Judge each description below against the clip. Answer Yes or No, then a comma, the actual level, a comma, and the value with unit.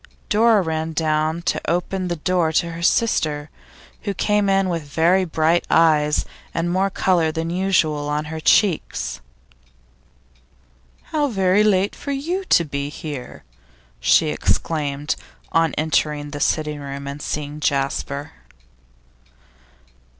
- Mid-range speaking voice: Yes, medium, 160 Hz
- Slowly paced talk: Yes, slow, 125 wpm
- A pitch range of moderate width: Yes, average, 3.8 semitones